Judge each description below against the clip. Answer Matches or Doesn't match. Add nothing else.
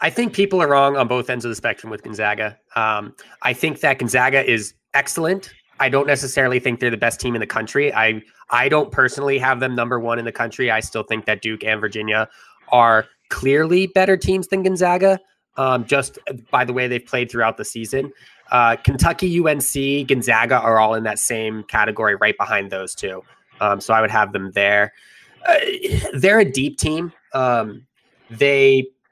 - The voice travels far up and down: Doesn't match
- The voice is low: Matches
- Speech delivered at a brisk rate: Doesn't match